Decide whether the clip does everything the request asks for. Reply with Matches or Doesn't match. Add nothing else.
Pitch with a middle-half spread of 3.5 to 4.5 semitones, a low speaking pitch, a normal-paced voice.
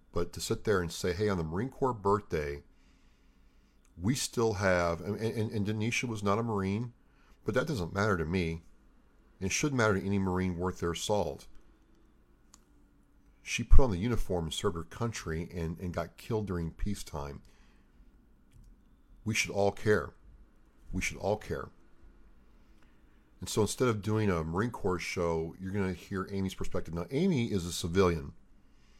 Matches